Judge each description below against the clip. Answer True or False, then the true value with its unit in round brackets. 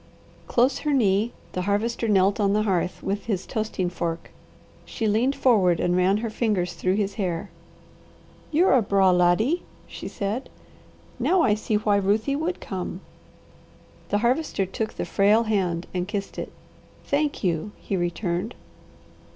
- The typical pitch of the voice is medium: False (205 Hz)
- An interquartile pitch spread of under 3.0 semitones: False (3.7 semitones)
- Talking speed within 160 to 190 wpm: False (150 wpm)